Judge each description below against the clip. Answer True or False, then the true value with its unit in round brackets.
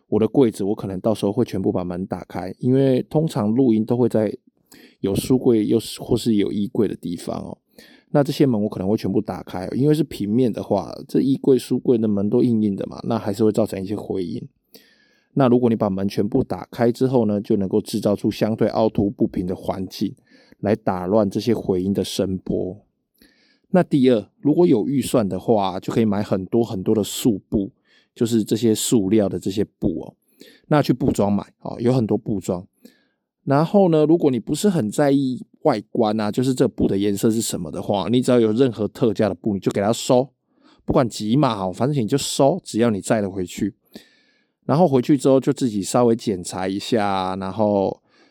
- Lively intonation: False (4.6 semitones)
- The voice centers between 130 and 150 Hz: False (115 Hz)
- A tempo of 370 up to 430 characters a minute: False (300 characters per minute)